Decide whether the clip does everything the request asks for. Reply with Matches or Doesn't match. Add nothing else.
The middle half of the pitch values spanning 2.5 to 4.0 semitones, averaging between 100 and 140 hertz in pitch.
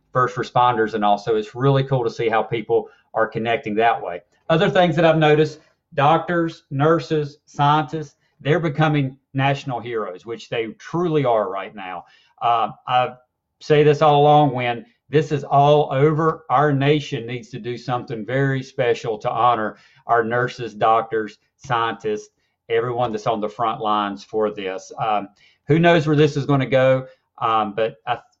Doesn't match